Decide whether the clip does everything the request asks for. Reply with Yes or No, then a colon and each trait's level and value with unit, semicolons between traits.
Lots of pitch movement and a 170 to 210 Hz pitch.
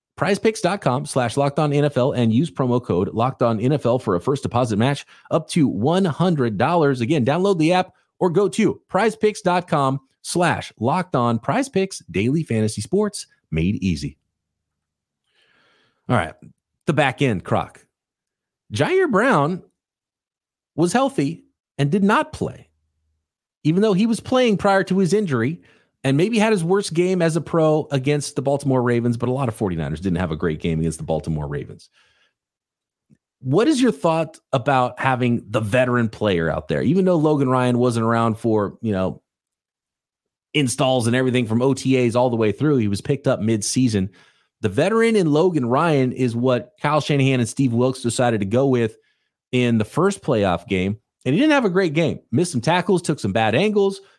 No: wide, 6.9 semitones; low, 130 Hz